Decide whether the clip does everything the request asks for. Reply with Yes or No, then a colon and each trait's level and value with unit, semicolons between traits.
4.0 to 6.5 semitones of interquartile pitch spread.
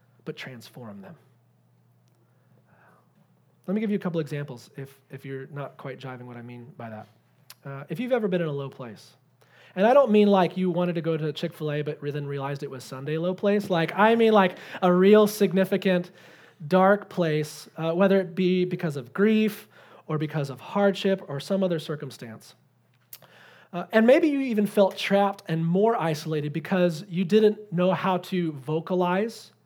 Yes: wide, 5.6 semitones